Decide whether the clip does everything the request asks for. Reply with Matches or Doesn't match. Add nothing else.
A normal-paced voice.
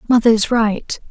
Matches